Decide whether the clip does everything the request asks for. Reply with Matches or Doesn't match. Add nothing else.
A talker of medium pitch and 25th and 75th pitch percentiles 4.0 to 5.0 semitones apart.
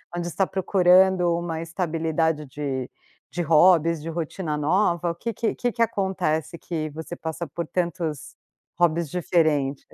Doesn't match